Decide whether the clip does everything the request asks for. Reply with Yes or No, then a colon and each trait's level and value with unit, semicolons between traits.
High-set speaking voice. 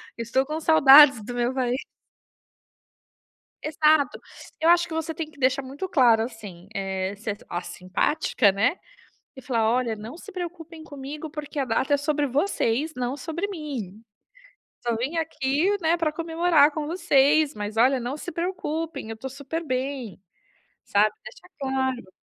Yes: very high, 275 Hz